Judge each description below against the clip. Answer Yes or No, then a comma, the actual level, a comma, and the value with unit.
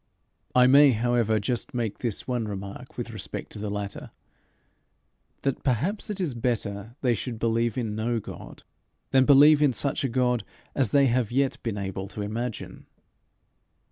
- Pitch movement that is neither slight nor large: Yes, average, 3.5 semitones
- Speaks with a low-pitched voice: Yes, low, 120 Hz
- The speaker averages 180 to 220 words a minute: No, average, 165 wpm